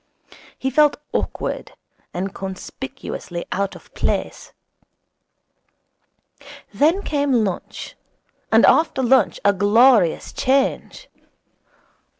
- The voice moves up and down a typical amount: No, wide, 5.9 semitones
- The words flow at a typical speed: No, slow, 85 wpm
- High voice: Yes, very high, 255 Hz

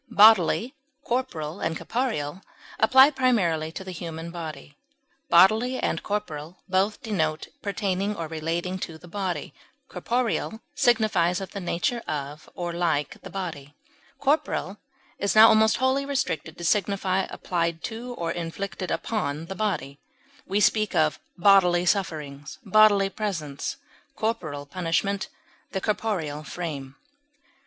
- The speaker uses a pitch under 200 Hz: Yes, medium, 185 Hz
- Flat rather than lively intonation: No, average, 4.9 semitones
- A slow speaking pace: Yes, slow, 125 wpm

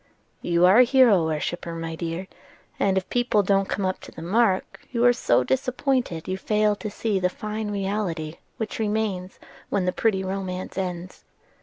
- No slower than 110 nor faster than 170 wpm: No, average, 180 wpm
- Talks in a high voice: Yes, high, 195 Hz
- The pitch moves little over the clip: No, average, 3.2 semitones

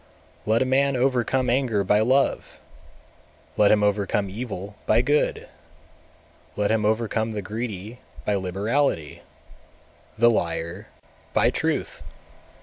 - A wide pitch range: No, average, 3.4 semitones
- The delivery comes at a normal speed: No, slow, 120 wpm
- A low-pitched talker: Yes, low, 110 Hz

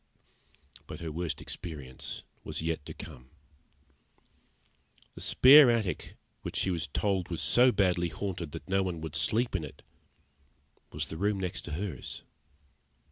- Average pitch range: Yes, average, 3.9 semitones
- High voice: No, very low, 90 Hz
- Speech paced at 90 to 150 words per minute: Yes, average, 145 wpm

